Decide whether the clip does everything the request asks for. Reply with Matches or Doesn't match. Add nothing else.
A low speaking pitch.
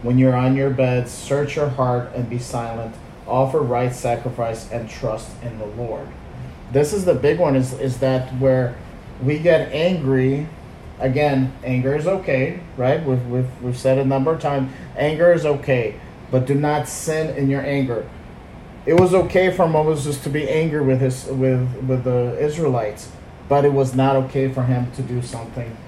Matches